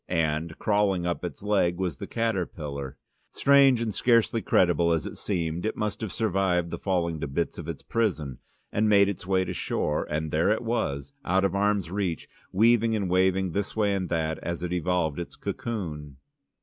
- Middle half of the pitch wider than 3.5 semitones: Yes, average, 4.0 semitones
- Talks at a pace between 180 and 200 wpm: Yes, average, 190 wpm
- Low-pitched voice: Yes, very low, 90 Hz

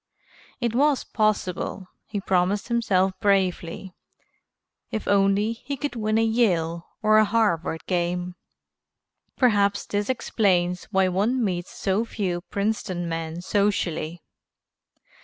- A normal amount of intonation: Yes, average, 3.5 semitones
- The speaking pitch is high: Yes, high, 200 Hz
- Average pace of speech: No, slow, 115 wpm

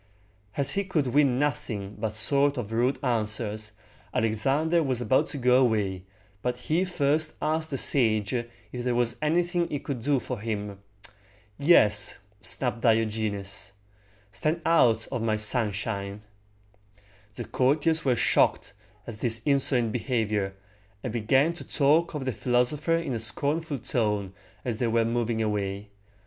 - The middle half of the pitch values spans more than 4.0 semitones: Yes, average, 4.8 semitones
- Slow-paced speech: No, average, 145 wpm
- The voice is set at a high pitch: No, low, 120 Hz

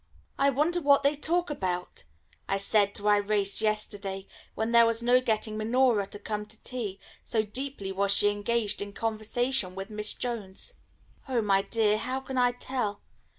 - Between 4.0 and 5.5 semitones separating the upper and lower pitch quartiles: No, average, 3.6 semitones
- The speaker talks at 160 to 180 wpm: Yes, average, 170 wpm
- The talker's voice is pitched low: No, high, 215 Hz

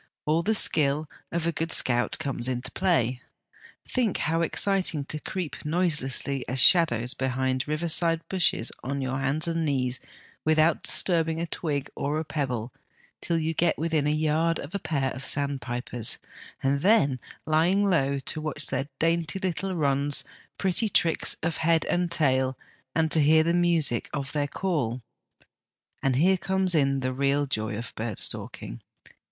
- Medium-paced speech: Yes, average, 160 wpm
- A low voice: No, medium, 155 Hz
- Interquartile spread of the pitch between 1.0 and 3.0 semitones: No, average, 3.8 semitones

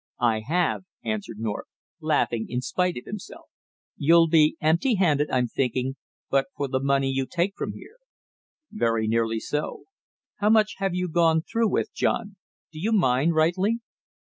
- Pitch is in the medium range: Yes, medium, 155 Hz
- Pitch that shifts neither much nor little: No, wide, 6.1 semitones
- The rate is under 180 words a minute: Yes, average, 160 wpm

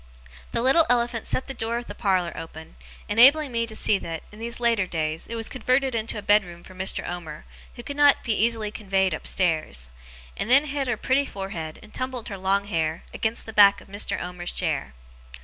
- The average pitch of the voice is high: Yes, high, 210 Hz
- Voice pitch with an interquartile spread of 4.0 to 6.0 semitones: Yes, average, 5.1 semitones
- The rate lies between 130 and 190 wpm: No, fast, 205 wpm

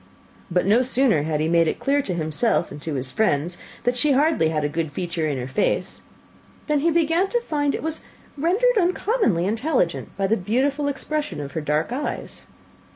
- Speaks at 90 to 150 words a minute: No, average, 190 wpm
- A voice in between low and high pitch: No, high, 225 Hz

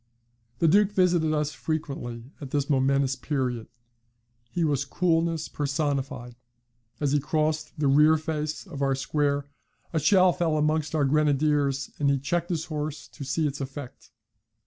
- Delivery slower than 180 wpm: Yes, average, 150 wpm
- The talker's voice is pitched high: No, medium, 150 Hz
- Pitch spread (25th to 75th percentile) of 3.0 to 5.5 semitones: No, narrow, 2.4 semitones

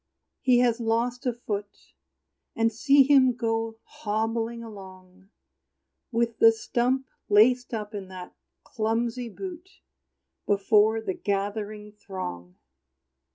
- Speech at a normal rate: No, slow, 110 wpm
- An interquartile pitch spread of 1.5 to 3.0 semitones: Yes, average, 2.7 semitones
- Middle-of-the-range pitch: No, high, 225 Hz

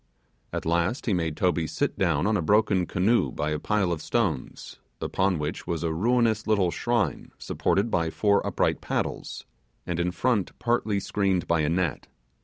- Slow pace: No, average, 175 wpm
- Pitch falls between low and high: No, very low, 95 Hz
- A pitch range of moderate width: Yes, average, 4.2 semitones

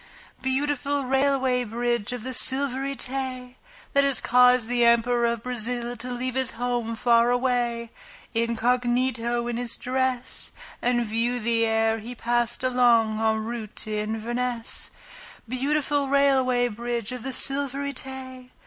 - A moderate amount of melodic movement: No, narrow, 1.8 semitones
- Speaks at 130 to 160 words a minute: Yes, slow, 135 wpm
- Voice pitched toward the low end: No, high, 245 Hz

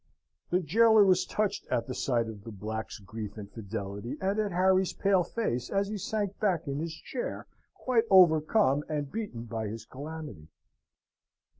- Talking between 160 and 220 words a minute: Yes, average, 165 wpm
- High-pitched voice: No, medium, 155 Hz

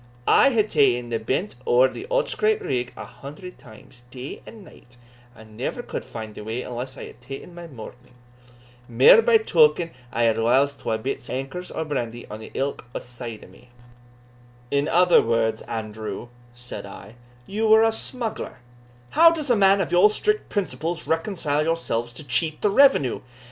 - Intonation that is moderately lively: No, wide, 8.5 semitones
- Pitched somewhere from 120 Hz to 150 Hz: Yes, medium, 140 Hz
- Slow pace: No, average, 175 wpm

